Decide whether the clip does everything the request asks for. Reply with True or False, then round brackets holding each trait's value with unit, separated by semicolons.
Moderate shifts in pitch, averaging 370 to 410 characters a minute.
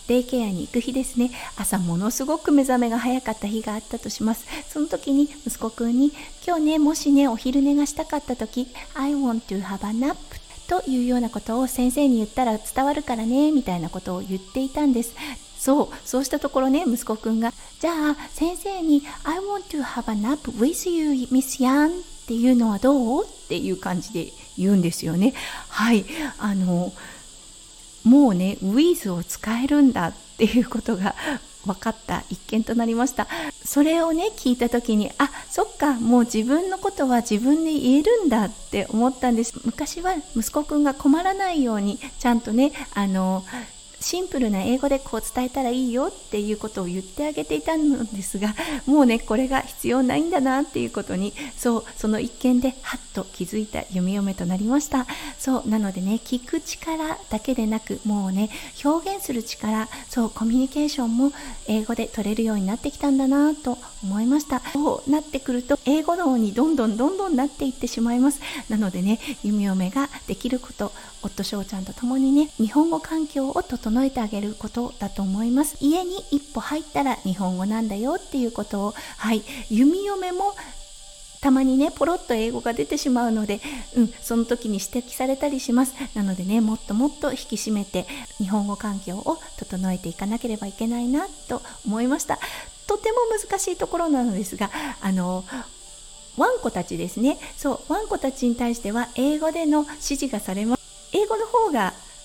True (5.0 semitones; 375 characters per minute)